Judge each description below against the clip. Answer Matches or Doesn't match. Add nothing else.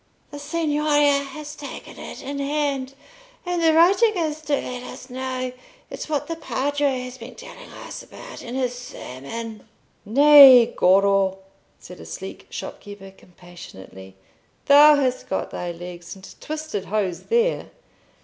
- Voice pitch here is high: Matches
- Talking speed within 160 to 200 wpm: Doesn't match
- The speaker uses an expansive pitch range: Matches